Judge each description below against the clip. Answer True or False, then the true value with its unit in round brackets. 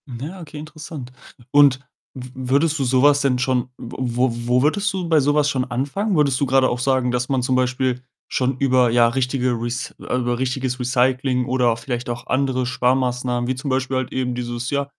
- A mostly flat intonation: True (1.9 semitones)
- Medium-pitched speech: False (130 Hz)